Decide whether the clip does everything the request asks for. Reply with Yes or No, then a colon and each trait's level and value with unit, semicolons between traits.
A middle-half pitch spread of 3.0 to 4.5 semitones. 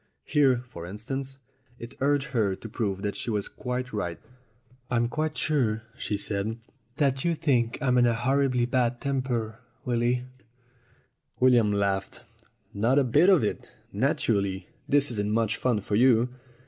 Yes: average, 3.8 semitones